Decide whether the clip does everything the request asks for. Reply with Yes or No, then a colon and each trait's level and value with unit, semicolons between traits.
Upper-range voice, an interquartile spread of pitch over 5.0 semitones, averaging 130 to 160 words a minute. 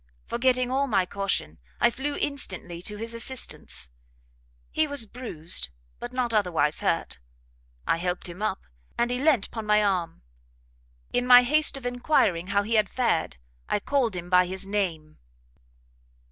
Yes: high, 210 Hz; wide, 5.6 semitones; average, 155 wpm